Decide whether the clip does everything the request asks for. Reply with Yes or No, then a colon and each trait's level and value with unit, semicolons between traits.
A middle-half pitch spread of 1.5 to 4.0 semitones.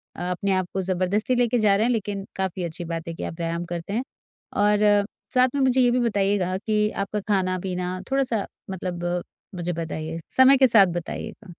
Yes: average, 3.5 semitones